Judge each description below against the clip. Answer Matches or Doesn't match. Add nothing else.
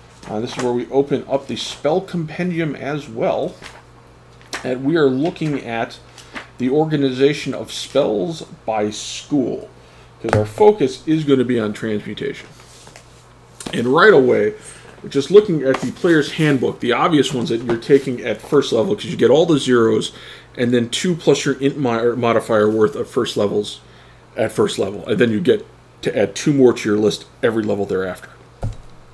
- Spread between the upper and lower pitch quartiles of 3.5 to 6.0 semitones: Matches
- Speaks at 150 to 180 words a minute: Matches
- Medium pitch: Doesn't match